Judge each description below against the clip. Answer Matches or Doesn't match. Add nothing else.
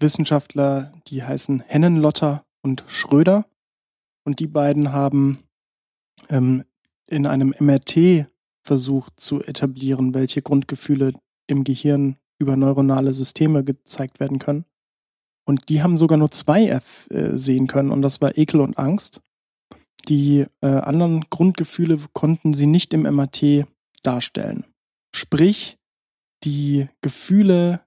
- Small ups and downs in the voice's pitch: Matches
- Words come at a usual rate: Doesn't match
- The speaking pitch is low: Doesn't match